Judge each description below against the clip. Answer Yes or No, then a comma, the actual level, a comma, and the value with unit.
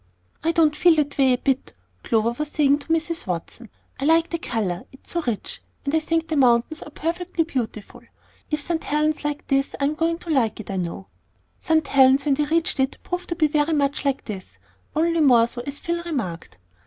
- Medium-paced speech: No, fast, 215 wpm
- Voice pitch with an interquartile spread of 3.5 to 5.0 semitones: Yes, average, 4.5 semitones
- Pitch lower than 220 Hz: No, very high, 290 Hz